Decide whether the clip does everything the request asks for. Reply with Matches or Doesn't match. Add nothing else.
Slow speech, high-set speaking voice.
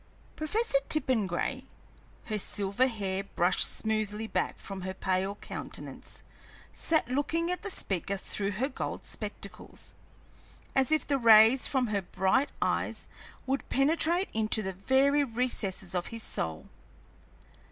Matches